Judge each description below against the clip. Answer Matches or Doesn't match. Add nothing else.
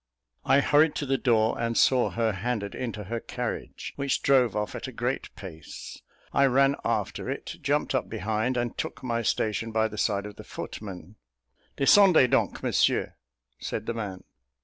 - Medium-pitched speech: Doesn't match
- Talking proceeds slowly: Doesn't match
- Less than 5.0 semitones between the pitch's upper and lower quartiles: Matches